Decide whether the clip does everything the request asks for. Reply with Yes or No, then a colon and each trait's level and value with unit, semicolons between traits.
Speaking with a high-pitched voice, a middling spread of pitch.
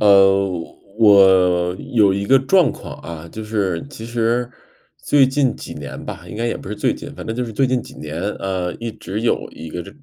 No: low, 105 Hz; average, 4.2 semitones